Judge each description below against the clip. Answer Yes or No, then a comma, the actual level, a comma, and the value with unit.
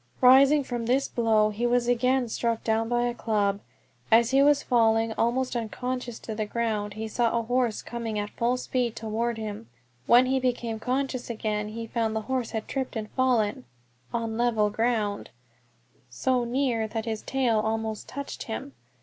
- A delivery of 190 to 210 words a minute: No, average, 175 wpm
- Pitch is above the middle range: Yes, high, 230 Hz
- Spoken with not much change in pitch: Yes, narrow, 2.3 semitones